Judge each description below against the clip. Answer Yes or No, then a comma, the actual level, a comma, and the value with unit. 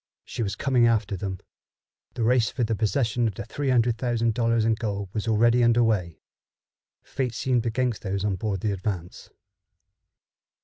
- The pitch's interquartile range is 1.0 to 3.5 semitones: Yes, average, 2.8 semitones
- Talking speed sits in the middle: Yes, average, 165 wpm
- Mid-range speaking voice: No, low, 115 Hz